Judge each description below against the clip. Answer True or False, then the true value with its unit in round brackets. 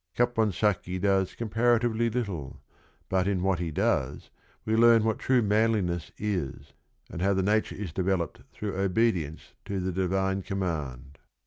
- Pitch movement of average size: True (3.7 semitones)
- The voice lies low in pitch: True (95 Hz)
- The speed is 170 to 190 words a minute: False (140 wpm)